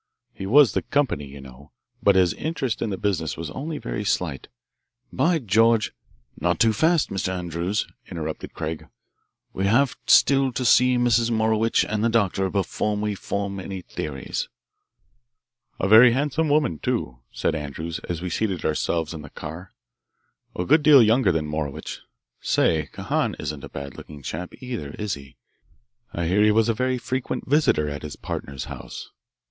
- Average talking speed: Yes, average, 170 wpm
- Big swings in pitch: Yes, wide, 7.0 semitones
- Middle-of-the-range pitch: No, low, 100 Hz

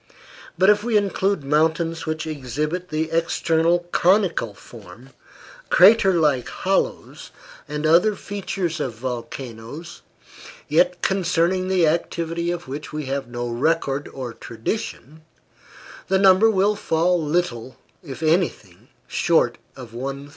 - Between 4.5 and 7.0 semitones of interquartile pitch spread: Yes, average, 5.0 semitones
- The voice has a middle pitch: Yes, medium, 160 Hz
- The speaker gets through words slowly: Yes, slow, 120 wpm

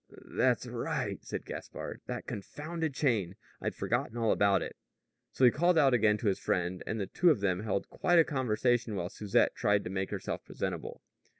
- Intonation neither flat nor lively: No, wide, 5.8 semitones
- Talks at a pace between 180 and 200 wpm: Yes, average, 190 wpm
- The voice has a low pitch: Yes, low, 110 Hz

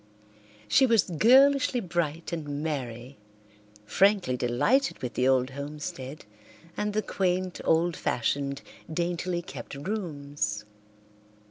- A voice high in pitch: No, medium, 160 Hz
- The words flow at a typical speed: No, slow, 105 wpm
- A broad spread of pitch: Yes, wide, 5.7 semitones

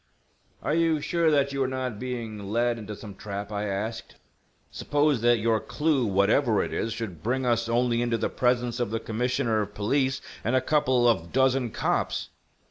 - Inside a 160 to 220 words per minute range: Yes, average, 185 wpm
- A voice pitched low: Yes, low, 120 Hz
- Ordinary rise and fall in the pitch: Yes, average, 3.3 semitones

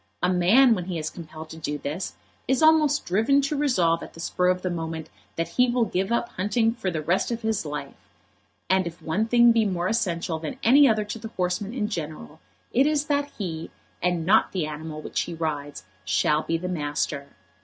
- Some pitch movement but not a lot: No, wide, 6.1 semitones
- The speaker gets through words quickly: Yes, fast, 210 wpm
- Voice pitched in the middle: Yes, medium, 180 Hz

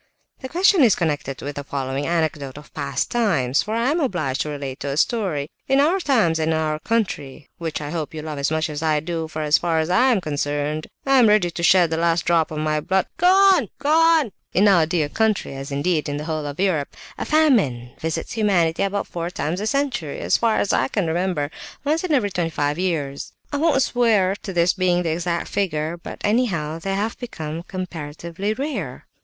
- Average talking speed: No, fast, 220 wpm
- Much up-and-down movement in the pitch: Yes, wide, 6.1 semitones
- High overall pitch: No, medium, 170 Hz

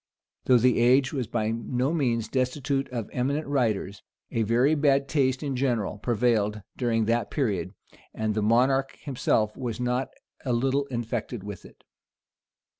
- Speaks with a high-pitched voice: No, low, 125 Hz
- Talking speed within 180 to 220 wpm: No, average, 150 wpm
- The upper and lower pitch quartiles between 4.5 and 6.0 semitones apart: No, average, 3.3 semitones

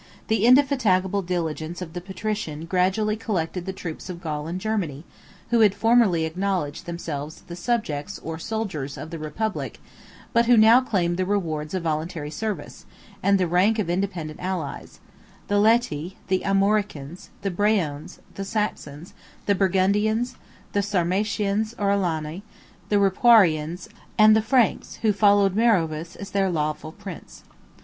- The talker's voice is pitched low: No, high, 190 Hz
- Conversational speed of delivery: Yes, average, 145 wpm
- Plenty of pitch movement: No, average, 4.4 semitones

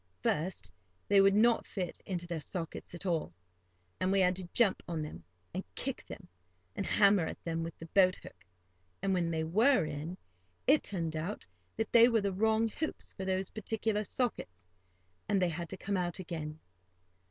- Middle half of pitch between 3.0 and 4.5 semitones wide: Yes, average, 3.7 semitones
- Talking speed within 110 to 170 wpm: No, average, 185 wpm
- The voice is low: No, medium, 185 Hz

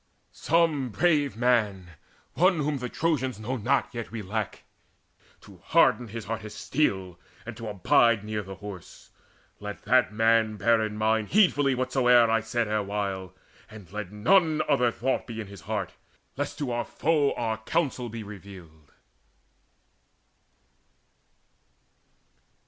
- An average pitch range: Yes, average, 3.8 semitones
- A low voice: Yes, low, 115 Hz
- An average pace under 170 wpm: Yes, average, 140 wpm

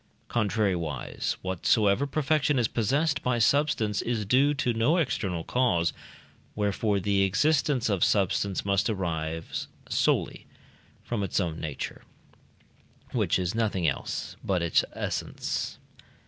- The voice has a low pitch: Yes, low, 105 Hz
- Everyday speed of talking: No, slow, 120 wpm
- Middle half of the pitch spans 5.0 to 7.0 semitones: Yes, wide, 5.4 semitones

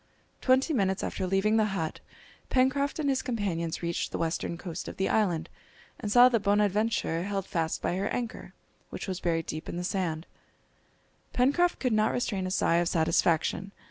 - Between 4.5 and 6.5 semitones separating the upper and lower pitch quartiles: Yes, average, 5.2 semitones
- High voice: Yes, high, 195 Hz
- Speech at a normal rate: Yes, average, 175 wpm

